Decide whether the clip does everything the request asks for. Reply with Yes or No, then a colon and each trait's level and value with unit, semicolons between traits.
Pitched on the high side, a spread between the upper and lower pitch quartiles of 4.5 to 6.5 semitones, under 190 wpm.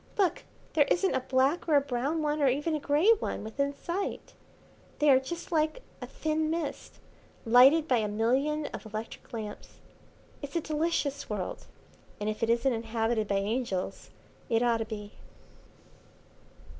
Yes: very high, 270 Hz; wide, 5.4 semitones; average, 160 wpm